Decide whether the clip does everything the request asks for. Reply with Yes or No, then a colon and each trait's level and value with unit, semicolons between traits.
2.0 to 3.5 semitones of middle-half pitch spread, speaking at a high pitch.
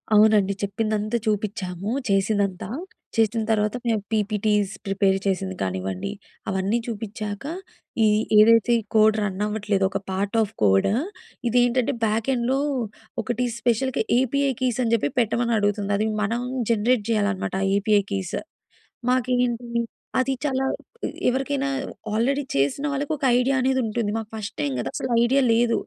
Yes: average, 3.1 semitones; high, 220 Hz